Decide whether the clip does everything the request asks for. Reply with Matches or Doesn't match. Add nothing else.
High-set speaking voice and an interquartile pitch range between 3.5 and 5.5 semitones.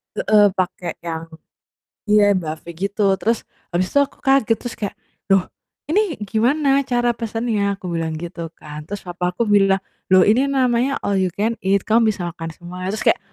Matches